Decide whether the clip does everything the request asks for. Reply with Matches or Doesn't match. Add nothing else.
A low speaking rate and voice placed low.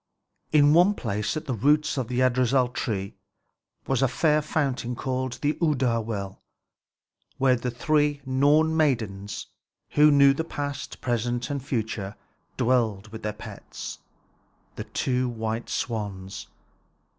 Matches